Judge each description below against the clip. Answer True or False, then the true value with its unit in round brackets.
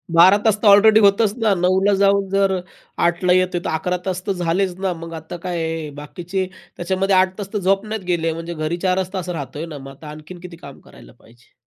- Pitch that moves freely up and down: False (2.9 semitones)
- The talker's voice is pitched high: False (180 Hz)